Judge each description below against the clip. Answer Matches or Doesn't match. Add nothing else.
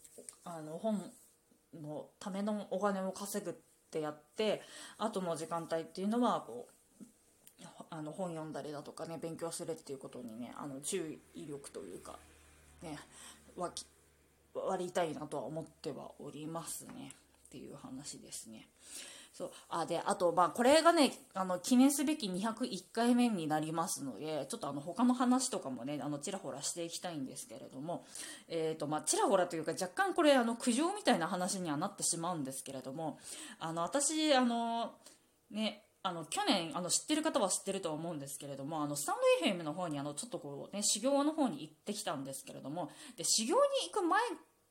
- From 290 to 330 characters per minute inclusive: Doesn't match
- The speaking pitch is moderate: Matches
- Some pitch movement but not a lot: Doesn't match